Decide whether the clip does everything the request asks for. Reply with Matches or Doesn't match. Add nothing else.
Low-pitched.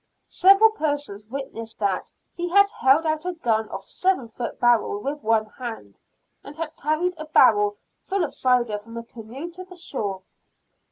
Doesn't match